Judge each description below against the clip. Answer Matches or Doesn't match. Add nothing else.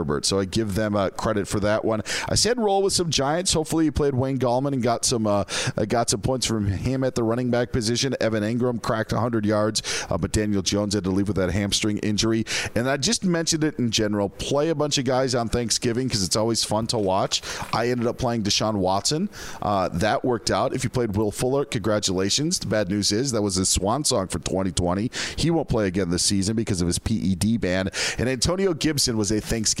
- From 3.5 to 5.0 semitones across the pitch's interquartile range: Matches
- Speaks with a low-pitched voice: Matches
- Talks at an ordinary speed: Doesn't match